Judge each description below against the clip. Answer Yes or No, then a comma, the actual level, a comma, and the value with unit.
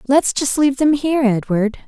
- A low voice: No, very high, 260 Hz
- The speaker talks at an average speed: Yes, average, 190 wpm